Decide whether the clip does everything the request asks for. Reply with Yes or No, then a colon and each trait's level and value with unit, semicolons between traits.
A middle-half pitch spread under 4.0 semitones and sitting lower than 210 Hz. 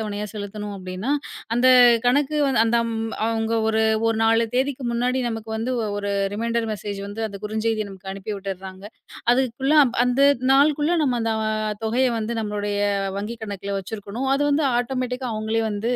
No: average, 3.3 semitones; high, 225 Hz